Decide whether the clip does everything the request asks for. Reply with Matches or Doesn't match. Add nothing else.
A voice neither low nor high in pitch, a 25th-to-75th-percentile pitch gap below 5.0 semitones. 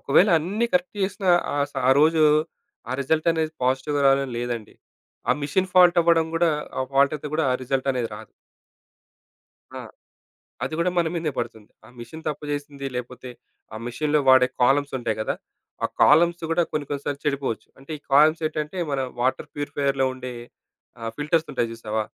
Matches